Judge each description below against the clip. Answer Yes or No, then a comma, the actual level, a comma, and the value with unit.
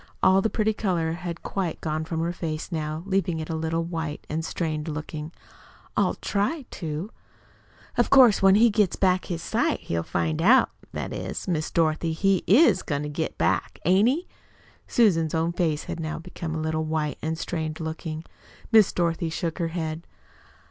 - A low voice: No, medium, 165 Hz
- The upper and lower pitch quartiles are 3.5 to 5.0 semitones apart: No, average, 3.1 semitones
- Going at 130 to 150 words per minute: No, average, 185 wpm